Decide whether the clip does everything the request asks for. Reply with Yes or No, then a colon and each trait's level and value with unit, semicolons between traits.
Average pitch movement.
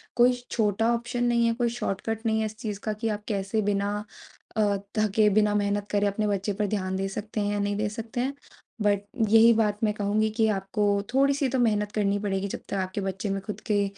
No: narrow, 1.7 semitones